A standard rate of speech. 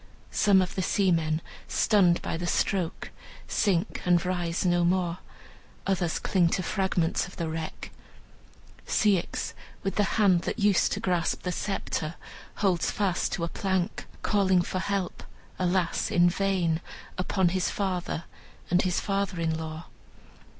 Yes: average, 145 wpm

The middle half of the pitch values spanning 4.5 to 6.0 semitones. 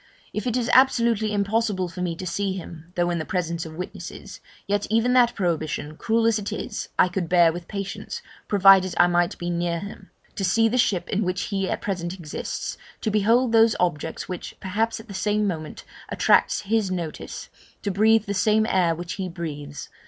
No: average, 3.7 semitones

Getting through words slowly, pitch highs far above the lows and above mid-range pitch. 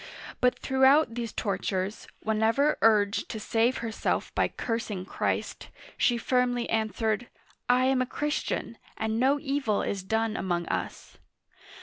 No: slow, 130 wpm; average, 2.8 semitones; high, 230 Hz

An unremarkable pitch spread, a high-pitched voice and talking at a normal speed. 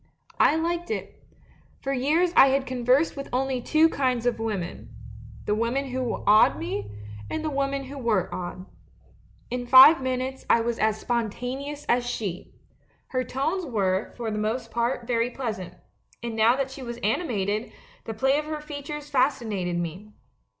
Yes: average, 4.0 semitones; very high, 250 Hz; average, 170 wpm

